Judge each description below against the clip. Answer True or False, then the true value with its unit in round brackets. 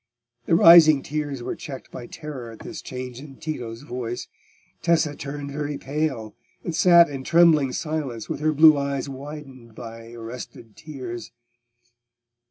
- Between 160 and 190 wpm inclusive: False (145 wpm)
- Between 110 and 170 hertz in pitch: True (140 Hz)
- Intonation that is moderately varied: True (3.8 semitones)